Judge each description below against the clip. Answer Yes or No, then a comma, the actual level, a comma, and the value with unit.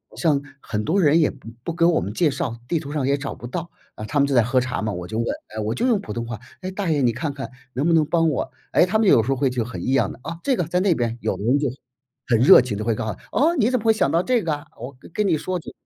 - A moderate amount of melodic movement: No, wide, 6.2 semitones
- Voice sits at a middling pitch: Yes, medium, 145 Hz